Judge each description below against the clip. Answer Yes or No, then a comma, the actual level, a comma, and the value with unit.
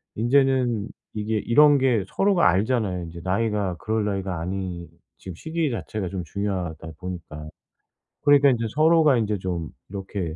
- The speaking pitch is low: Yes, low, 105 Hz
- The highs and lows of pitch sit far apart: Yes, wide, 5.7 semitones